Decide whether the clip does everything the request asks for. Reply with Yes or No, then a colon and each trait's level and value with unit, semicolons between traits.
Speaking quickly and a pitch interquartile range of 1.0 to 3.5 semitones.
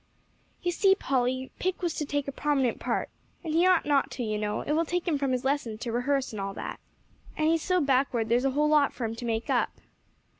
No: fast, 240 wpm; average, 4.3 semitones